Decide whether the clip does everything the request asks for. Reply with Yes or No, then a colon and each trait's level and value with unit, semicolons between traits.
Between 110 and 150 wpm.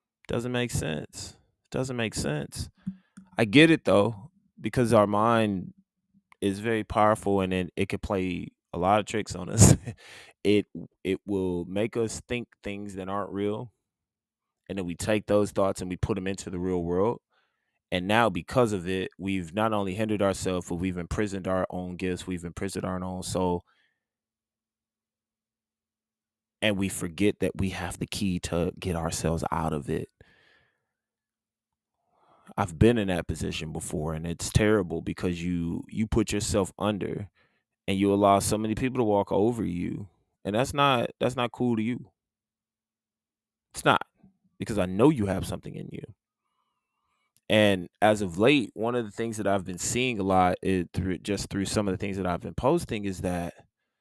No: average, 175 wpm